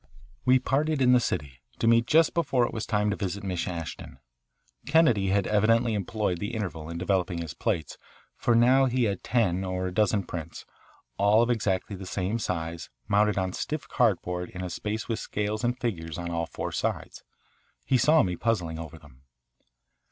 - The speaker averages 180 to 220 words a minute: Yes, average, 185 wpm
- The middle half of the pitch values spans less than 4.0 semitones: No, average, 4.8 semitones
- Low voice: Yes, low, 100 Hz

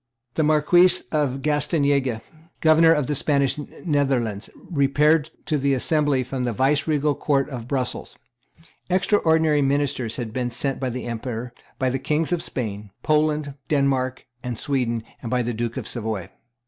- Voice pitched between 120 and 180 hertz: Yes, medium, 140 Hz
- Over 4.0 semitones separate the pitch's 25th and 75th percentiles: No, average, 3.4 semitones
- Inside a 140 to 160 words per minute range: Yes, average, 150 wpm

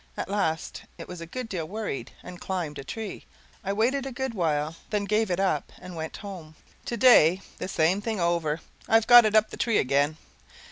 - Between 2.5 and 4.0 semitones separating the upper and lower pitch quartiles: No, average, 5.3 semitones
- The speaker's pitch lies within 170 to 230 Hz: Yes, medium, 185 Hz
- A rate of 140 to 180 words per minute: No, average, 200 wpm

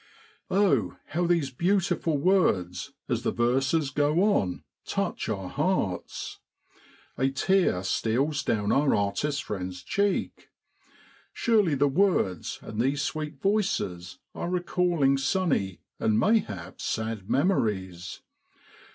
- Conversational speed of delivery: No, slow, 110 wpm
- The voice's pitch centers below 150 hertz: Yes, medium, 140 Hz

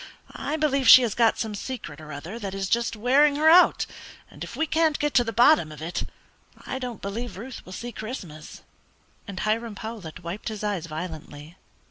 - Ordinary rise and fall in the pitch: No, wide, 5.9 semitones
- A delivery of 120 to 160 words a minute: No, average, 195 wpm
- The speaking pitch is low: No, high, 220 Hz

